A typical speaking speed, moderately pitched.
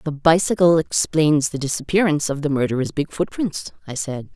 Yes: average, 180 wpm; medium, 155 Hz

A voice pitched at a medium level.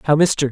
Yes: medium, 145 Hz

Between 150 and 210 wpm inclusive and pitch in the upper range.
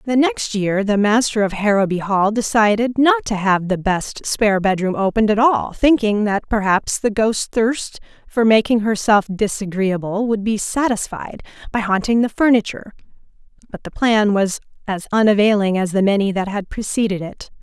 Yes: average, 165 wpm; high, 210 Hz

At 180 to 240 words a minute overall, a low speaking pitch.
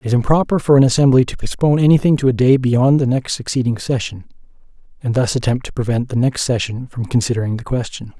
Yes: fast, 205 wpm; low, 125 Hz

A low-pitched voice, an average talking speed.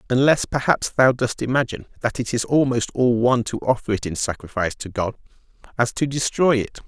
Yes: low, 120 Hz; average, 190 wpm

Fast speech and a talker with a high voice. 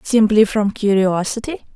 No: slow, 105 wpm; high, 210 Hz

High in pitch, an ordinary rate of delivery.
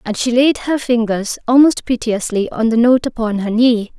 Yes: high, 235 Hz; average, 195 wpm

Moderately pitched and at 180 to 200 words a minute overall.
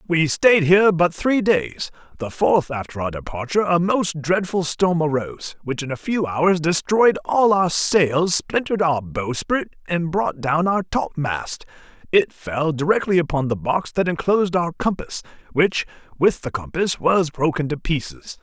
No: medium, 165 Hz; average, 165 wpm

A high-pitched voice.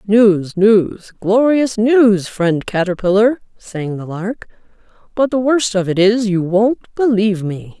Yes: high, 210 Hz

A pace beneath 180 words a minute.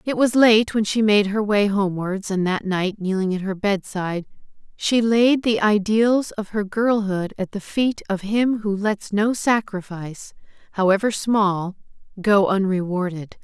Yes: average, 160 wpm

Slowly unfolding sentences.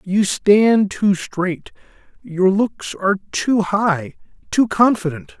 Yes: slow, 120 wpm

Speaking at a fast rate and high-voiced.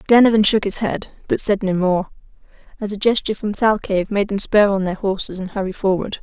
Yes: fast, 210 wpm; high, 200 Hz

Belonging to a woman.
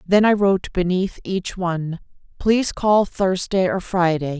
Yes: female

